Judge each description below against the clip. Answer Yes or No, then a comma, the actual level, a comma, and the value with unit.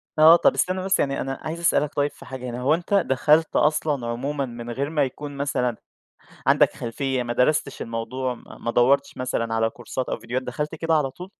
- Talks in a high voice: No, low, 135 Hz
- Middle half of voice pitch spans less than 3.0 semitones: No, average, 3.7 semitones